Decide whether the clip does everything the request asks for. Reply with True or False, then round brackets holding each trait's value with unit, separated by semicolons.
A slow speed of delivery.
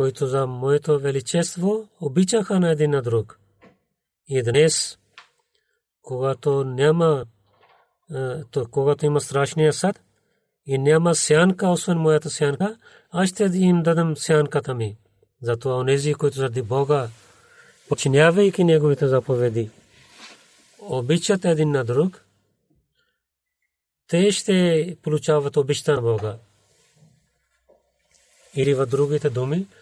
True (105 wpm)